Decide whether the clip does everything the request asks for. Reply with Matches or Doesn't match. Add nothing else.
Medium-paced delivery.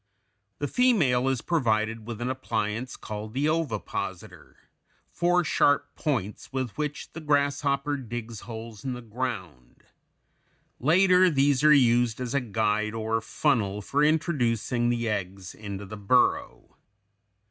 Doesn't match